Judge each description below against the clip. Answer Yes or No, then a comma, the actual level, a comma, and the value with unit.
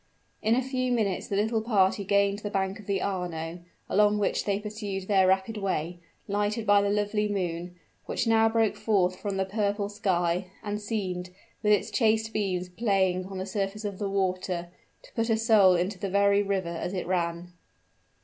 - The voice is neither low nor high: No, high, 200 Hz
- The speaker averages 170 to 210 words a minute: Yes, average, 190 wpm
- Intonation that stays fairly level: Yes, narrow, 2.2 semitones